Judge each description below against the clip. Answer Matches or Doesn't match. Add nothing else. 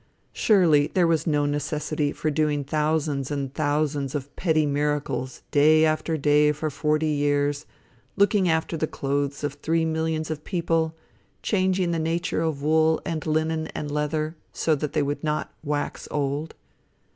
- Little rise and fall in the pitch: Matches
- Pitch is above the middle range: Doesn't match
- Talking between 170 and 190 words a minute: Doesn't match